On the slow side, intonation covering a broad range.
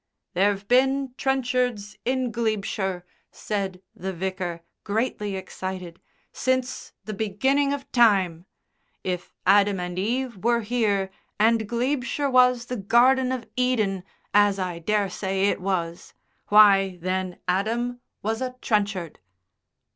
No: slow, 115 wpm; average, 4.6 semitones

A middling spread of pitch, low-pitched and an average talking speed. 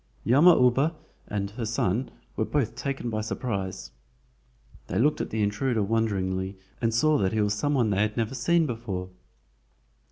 Yes: average, 4.0 semitones; low, 115 Hz; average, 165 wpm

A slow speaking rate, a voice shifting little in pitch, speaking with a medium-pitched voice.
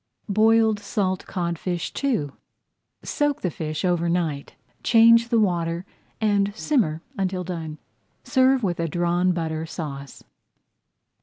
No: slow, 120 wpm; average, 4.7 semitones; medium, 180 Hz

